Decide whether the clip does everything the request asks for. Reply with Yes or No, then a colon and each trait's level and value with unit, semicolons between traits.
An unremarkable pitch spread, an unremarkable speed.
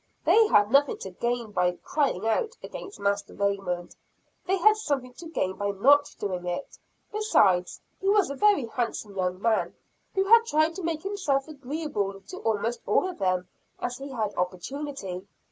No: wide, 8.4 semitones; average, 170 wpm